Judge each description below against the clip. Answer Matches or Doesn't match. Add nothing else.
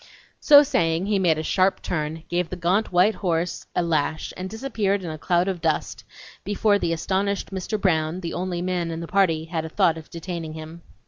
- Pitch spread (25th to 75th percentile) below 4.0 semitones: Matches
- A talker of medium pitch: Matches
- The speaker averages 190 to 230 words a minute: Matches